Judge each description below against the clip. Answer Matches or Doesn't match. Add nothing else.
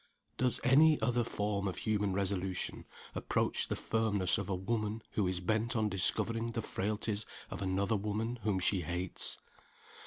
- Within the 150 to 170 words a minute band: Matches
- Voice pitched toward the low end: Matches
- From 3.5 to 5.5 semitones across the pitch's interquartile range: Doesn't match